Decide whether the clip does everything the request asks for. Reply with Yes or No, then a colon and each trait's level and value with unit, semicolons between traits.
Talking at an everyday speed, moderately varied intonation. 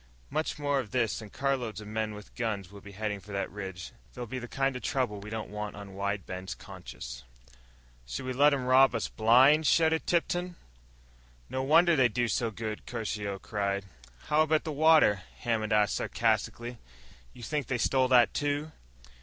Yes: average, 185 wpm; average, 4.8 semitones